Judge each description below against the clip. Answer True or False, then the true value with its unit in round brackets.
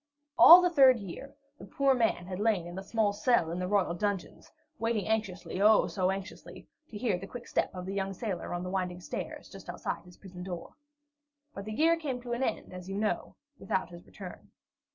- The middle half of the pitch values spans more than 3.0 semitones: True (3.8 semitones)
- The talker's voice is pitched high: True (195 Hz)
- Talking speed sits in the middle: False (215 wpm)